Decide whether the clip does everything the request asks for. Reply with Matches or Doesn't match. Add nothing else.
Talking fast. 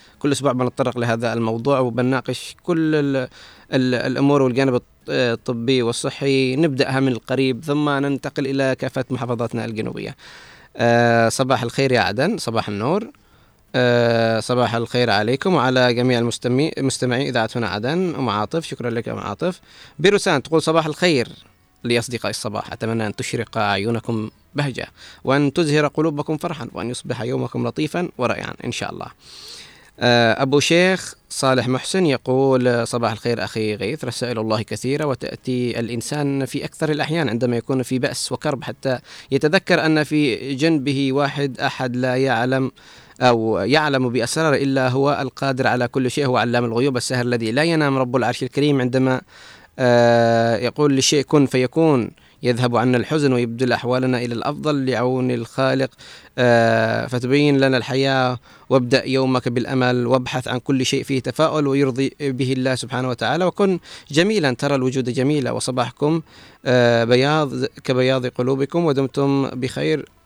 Matches